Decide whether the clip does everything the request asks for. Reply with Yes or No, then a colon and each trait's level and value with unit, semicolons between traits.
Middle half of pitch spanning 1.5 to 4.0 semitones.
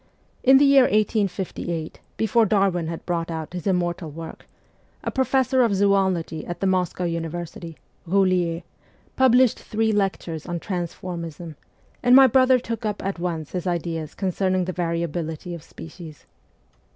Yes: average, 3.7 semitones